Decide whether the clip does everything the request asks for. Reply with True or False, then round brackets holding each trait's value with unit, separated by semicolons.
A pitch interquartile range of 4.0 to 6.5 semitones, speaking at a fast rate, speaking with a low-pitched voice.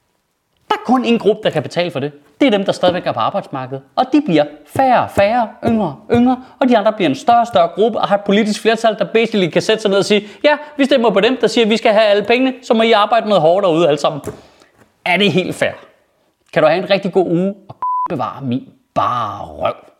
False (4.5 semitones; 245 wpm; 210 Hz)